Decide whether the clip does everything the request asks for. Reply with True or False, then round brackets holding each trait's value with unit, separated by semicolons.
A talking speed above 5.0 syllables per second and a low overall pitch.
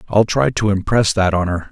True (5.2 syllables/s; 100 Hz)